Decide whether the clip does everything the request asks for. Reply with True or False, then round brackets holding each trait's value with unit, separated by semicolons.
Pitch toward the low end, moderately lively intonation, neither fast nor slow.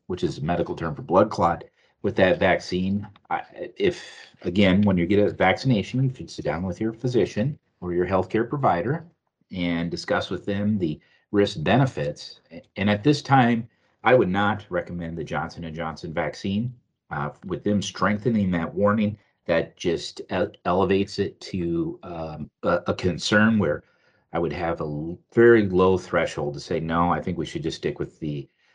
True (100 Hz; 3.9 semitones; 170 wpm)